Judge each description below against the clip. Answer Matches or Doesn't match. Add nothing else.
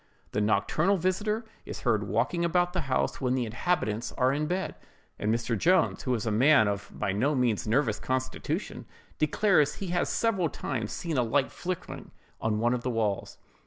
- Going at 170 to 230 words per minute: Matches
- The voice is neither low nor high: Doesn't match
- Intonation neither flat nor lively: Doesn't match